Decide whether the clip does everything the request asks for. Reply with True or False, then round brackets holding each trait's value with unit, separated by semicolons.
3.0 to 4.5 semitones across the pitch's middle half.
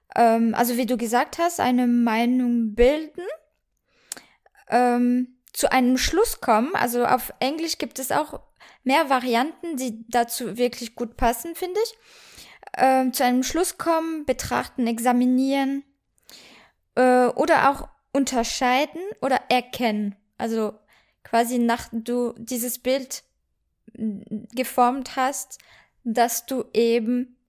False (2.5 semitones)